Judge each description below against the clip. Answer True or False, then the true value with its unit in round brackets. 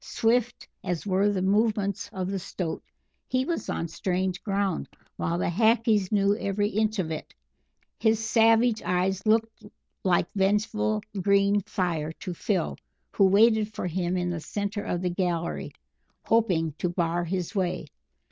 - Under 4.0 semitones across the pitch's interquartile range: True (3.3 semitones)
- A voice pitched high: True (195 Hz)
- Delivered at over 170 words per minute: False (150 wpm)